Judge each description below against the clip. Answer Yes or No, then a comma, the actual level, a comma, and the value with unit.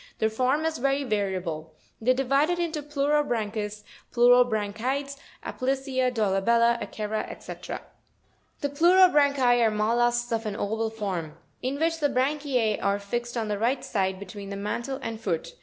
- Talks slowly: No, average, 165 wpm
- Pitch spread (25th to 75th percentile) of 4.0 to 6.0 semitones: Yes, average, 4.6 semitones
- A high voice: Yes, high, 240 Hz